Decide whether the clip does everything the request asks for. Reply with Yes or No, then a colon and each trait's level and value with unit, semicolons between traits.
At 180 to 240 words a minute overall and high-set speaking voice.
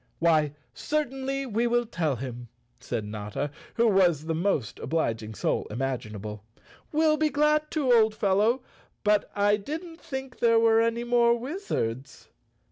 No: average, 140 wpm; high, 215 Hz